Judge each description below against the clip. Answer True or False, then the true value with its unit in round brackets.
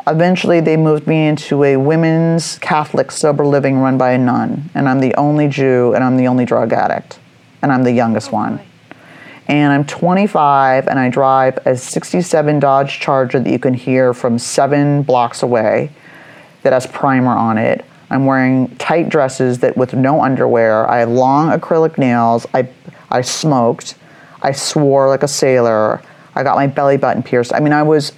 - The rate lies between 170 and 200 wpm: True (180 wpm)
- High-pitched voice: False (135 Hz)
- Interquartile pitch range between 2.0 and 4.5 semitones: True (2.7 semitones)